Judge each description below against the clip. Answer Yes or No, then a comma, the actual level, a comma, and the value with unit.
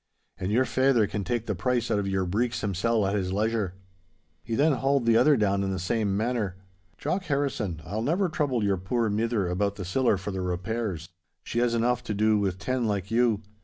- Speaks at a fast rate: Yes, fast, 210 wpm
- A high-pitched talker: No, low, 110 Hz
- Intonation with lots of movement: No, average, 3.8 semitones